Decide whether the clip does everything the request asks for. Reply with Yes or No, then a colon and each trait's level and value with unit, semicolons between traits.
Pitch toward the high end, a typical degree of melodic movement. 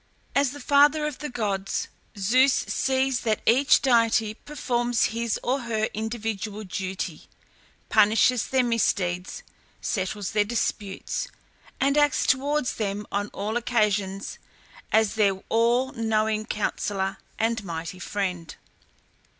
Yes: high, 220 Hz; average, 3.8 semitones